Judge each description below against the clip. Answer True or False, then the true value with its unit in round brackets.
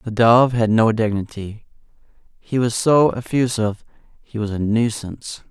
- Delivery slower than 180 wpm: True (140 wpm)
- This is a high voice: False (115 Hz)